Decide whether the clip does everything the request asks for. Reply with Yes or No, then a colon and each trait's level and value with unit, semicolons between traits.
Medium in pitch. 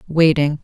Yes: medium, 155 Hz